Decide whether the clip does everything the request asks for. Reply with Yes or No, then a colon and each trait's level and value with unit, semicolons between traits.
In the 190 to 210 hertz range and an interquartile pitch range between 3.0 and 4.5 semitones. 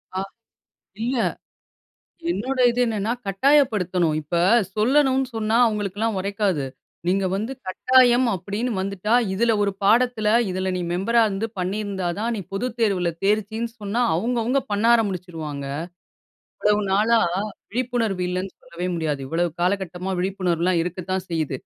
Yes: high, 200 Hz; average, 4.0 semitones